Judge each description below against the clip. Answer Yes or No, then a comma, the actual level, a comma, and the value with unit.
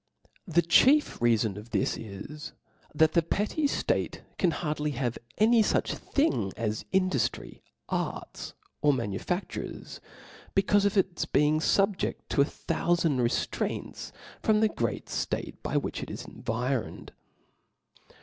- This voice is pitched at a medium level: Yes, medium, 155 Hz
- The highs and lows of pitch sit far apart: Yes, wide, 8.5 semitones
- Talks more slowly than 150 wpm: Yes, slow, 135 wpm